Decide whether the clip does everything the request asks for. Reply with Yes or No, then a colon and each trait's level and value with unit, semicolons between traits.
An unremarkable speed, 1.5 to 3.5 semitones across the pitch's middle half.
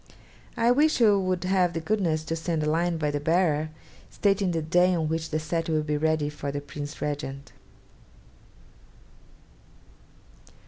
Yes: average, 155 wpm; average, 3.2 semitones